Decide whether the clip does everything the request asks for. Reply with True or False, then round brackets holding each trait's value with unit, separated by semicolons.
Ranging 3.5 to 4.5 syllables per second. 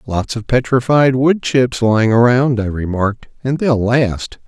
True (4.3 syllables/s)